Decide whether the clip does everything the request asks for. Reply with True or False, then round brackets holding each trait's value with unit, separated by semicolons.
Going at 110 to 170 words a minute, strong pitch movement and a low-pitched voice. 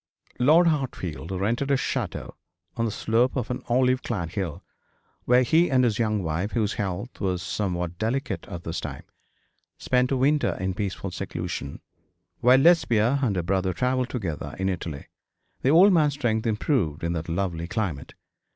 True (165 wpm; 6.0 semitones; 110 Hz)